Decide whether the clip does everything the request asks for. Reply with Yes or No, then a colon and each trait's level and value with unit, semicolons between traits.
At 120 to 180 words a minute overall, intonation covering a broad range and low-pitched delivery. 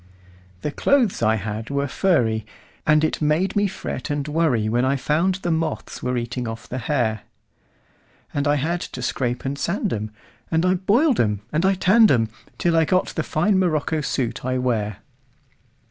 No: average, 160 wpm; wide, 6.5 semitones; medium, 145 Hz